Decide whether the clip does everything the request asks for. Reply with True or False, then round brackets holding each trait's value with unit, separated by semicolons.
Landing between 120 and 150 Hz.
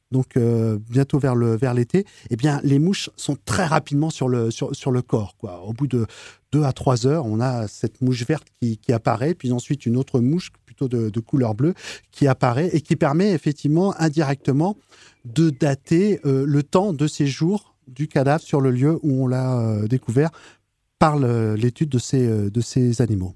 True (135 Hz)